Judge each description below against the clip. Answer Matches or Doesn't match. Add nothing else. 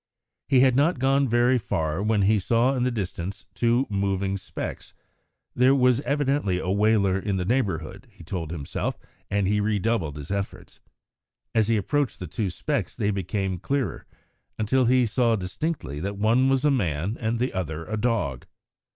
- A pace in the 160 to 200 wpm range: Matches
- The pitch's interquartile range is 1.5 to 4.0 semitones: Doesn't match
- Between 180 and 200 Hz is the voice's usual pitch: Doesn't match